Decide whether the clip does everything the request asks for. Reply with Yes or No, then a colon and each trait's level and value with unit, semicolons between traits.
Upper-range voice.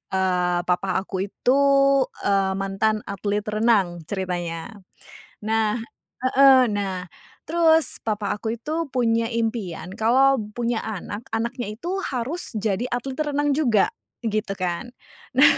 Yes: high, 220 Hz